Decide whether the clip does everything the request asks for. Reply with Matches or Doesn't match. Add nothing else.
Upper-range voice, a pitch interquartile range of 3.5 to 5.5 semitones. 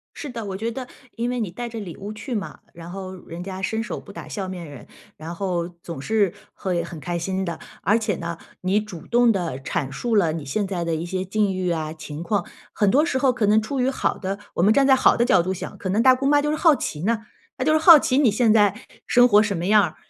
Matches